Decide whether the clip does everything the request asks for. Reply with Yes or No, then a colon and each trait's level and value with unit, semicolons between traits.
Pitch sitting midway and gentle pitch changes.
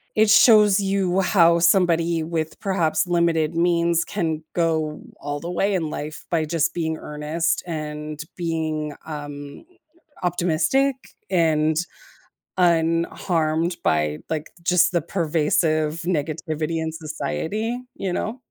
Yes: medium, 165 Hz; narrow, 2.3 semitones